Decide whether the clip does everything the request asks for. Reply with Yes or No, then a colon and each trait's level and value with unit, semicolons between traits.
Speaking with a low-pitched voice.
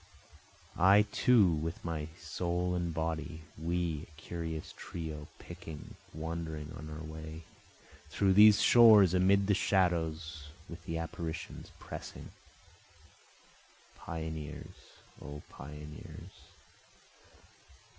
Yes: very low, 80 Hz